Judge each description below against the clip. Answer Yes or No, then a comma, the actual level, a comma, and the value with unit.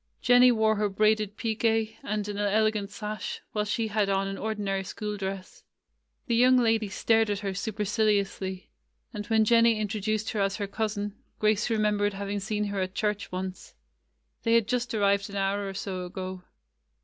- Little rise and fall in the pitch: Yes, narrow, 1.8 semitones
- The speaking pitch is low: No, high, 210 Hz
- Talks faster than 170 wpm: Yes, average, 180 wpm